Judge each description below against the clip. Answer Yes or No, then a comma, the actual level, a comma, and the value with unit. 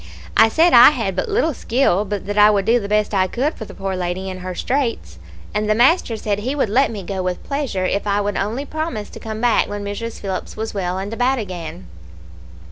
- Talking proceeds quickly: Yes, fast, 235 wpm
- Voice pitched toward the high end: Yes, high, 210 Hz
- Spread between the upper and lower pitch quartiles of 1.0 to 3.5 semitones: No, average, 4.0 semitones